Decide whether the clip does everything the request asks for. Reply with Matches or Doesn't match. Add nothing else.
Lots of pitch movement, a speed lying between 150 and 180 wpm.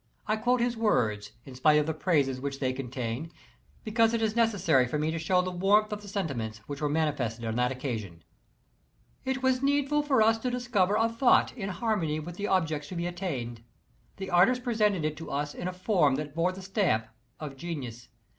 Doesn't match